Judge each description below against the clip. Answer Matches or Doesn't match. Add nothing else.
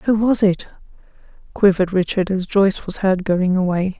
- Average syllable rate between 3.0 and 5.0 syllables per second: Doesn't match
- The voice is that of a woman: Matches